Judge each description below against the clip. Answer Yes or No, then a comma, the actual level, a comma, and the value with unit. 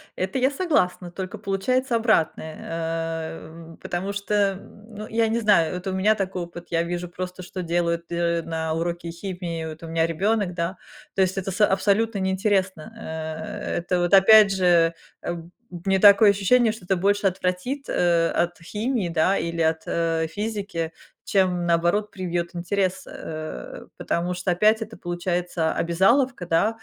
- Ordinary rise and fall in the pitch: Yes, average, 3.1 semitones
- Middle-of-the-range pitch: Yes, medium, 180 Hz